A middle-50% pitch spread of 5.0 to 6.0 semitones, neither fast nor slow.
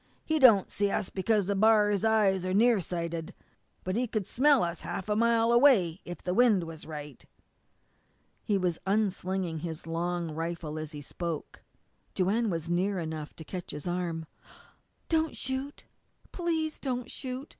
Yes: average, 5.3 semitones; average, 160 wpm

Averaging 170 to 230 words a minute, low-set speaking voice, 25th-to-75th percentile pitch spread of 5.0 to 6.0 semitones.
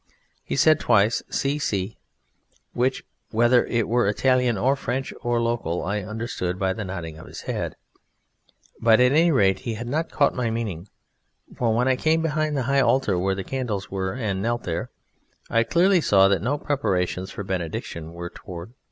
Yes: average, 180 wpm; low, 115 Hz; average, 5.3 semitones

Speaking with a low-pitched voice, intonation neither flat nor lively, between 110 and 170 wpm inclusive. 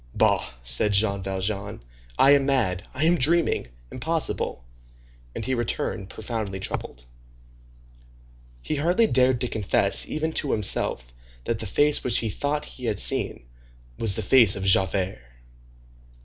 No: low, 110 Hz; wide, 6.1 semitones; average, 140 wpm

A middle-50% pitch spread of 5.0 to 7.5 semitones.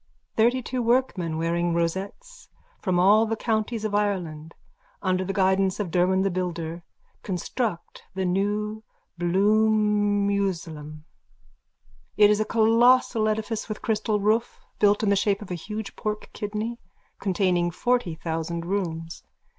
No: average, 3.6 semitones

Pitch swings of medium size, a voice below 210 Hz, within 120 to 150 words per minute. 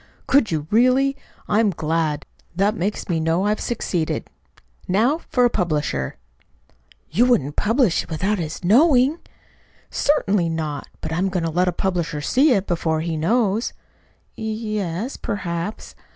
No: wide, 5.8 semitones; high, 190 Hz; average, 145 wpm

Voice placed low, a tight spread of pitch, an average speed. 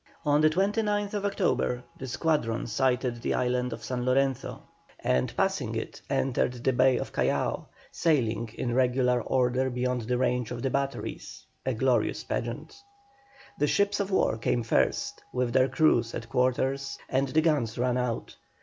Yes: low, 130 Hz; narrow, 2.0 semitones; average, 160 wpm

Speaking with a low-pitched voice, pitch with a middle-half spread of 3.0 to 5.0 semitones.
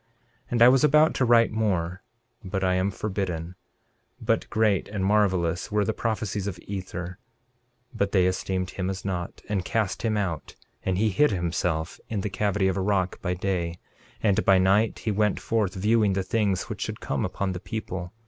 No: very low, 95 Hz; narrow, 2.5 semitones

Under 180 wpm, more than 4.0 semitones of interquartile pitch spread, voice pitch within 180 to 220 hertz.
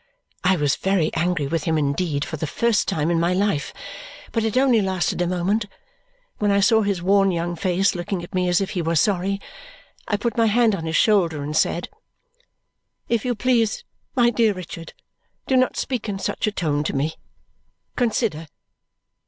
No: average, 185 wpm; average, 4.5 semitones; high, 190 Hz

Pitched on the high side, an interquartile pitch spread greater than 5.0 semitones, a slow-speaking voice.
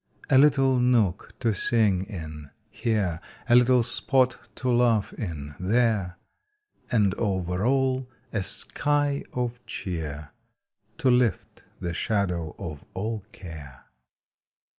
No: low, 105 Hz; wide, 5.6 semitones; slow, 115 wpm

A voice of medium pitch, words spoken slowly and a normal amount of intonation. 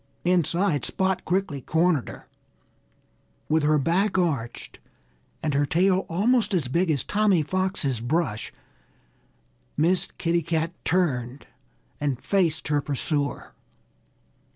Yes: medium, 165 Hz; slow, 110 wpm; average, 4.3 semitones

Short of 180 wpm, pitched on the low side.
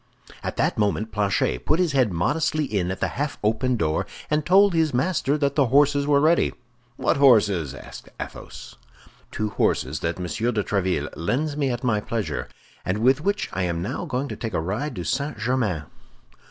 No: average, 190 wpm; low, 120 Hz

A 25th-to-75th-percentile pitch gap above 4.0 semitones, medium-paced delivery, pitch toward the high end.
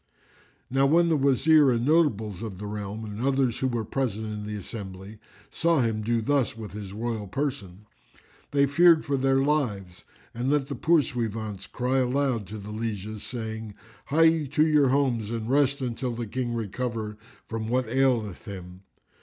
No: average, 4.5 semitones; average, 170 wpm; low, 120 Hz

